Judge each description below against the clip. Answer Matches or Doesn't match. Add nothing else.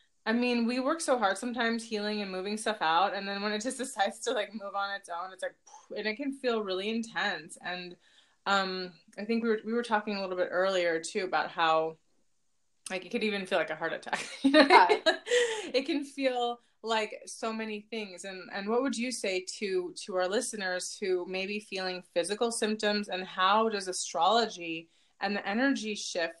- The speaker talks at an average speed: Doesn't match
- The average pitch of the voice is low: Doesn't match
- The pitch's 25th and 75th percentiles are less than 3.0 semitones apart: Doesn't match